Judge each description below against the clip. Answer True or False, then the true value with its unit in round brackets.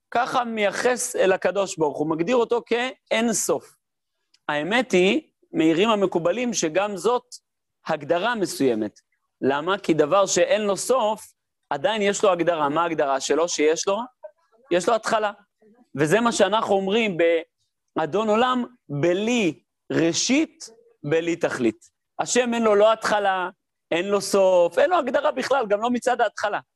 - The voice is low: False (205 Hz)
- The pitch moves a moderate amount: False (5.9 semitones)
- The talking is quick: False (140 wpm)